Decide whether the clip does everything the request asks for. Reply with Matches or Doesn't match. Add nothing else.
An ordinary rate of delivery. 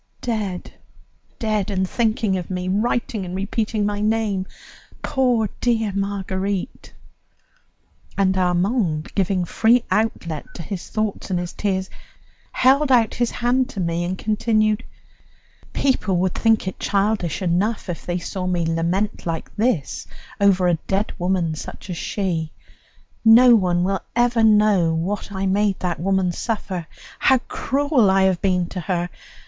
Matches